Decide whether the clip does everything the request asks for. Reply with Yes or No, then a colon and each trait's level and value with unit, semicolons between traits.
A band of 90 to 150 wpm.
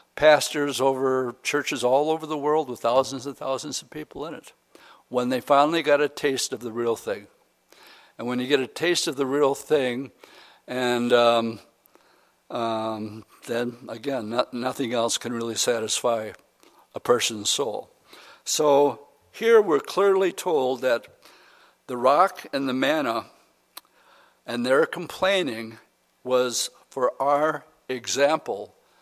Yes: average, 140 wpm